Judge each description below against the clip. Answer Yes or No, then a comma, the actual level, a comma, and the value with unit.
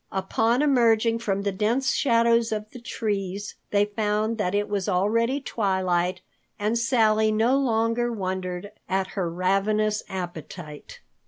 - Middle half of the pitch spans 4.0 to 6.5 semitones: No, average, 3.3 semitones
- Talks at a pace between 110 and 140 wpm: Yes, slow, 135 wpm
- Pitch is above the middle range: Yes, high, 210 Hz